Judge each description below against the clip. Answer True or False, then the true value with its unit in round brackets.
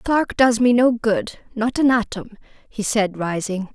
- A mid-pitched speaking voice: False (225 Hz)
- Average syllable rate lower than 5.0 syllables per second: True (4.5 syllables/s)